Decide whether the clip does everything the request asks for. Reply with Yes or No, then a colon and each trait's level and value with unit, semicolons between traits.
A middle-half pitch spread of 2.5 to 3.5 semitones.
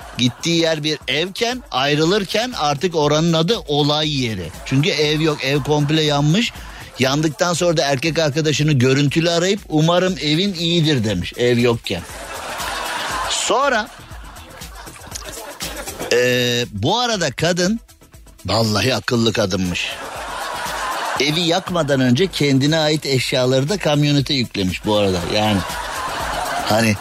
No: average, 5.2 semitones